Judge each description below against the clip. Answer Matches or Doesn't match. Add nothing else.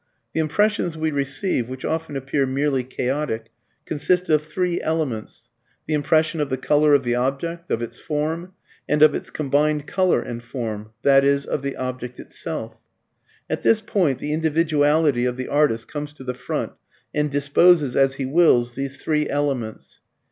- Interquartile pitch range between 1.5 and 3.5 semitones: Matches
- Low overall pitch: Doesn't match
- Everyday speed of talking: Matches